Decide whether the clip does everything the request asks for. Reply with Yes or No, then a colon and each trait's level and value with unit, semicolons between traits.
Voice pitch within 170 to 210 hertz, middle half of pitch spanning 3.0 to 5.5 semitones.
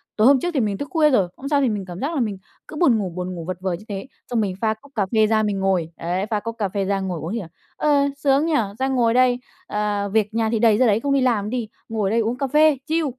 No: high, 220 Hz; average, 4.8 semitones